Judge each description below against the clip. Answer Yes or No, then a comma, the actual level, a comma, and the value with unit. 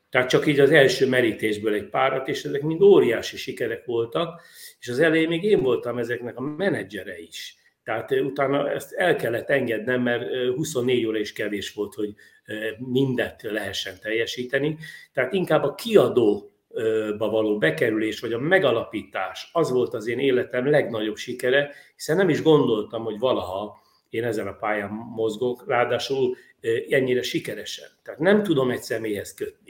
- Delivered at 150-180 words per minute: Yes, fast, 155 wpm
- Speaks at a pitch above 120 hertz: Yes, low, 130 Hz